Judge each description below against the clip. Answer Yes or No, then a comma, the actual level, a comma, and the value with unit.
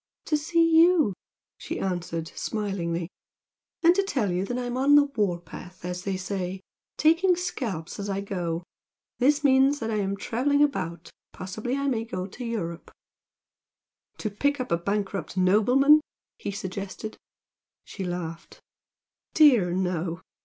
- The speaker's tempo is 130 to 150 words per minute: Yes, average, 145 wpm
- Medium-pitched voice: No, high, 205 Hz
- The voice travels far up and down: Yes, wide, 7.3 semitones